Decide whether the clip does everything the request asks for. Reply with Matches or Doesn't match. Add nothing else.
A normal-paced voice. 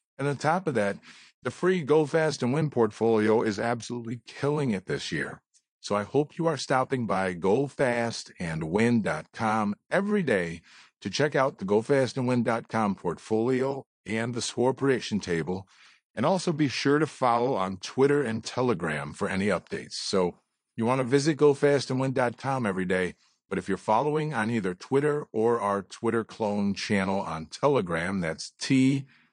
Matches